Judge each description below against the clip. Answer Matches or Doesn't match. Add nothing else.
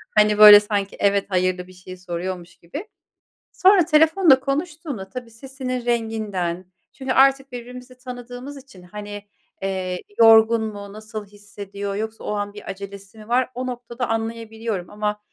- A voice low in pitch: Doesn't match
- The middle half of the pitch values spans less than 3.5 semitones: Doesn't match